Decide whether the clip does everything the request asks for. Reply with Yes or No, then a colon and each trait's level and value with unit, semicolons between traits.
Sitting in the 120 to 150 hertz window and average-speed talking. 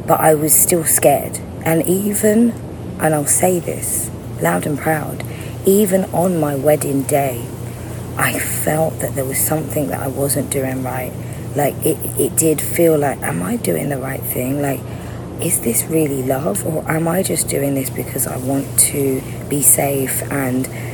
Yes: low, 135 Hz; average, 170 wpm